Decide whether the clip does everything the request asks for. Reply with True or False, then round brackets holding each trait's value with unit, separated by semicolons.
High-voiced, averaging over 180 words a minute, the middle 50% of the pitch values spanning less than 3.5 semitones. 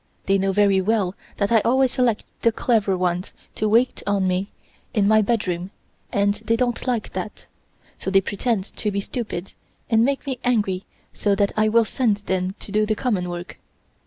True (205 Hz; 190 wpm; 3.0 semitones)